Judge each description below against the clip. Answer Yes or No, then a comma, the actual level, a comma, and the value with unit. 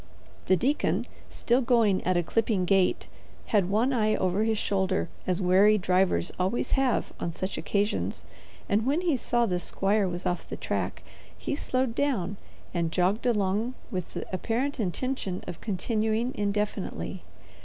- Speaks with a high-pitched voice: Yes, high, 205 Hz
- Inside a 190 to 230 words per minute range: No, average, 155 wpm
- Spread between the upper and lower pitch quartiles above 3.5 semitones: Yes, average, 4.2 semitones